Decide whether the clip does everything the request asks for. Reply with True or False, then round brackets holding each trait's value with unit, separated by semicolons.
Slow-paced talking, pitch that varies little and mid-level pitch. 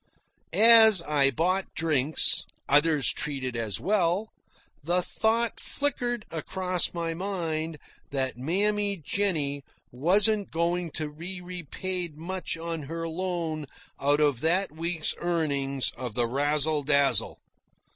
False (115 wpm; 4.3 semitones; 165 Hz)